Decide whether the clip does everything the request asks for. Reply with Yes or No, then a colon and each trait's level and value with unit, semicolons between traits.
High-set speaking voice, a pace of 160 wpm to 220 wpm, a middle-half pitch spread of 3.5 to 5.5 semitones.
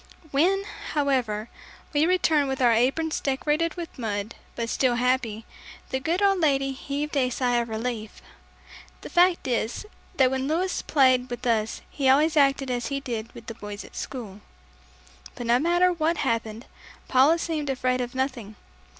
Yes: very high, 265 Hz; average, 165 wpm; average, 4.1 semitones